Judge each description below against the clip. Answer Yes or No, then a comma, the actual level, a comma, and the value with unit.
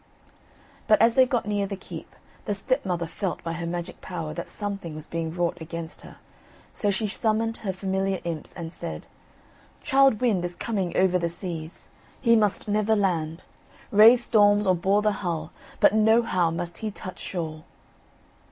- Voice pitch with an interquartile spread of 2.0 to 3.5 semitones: No, average, 3.9 semitones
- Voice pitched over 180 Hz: Yes, high, 190 Hz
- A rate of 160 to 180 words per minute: Yes, average, 170 wpm